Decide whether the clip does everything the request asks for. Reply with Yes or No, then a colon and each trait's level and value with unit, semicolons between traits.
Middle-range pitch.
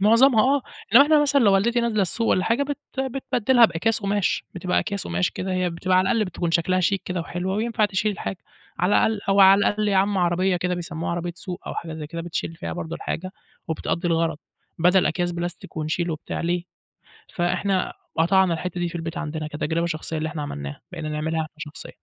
Yes: medium, 180 Hz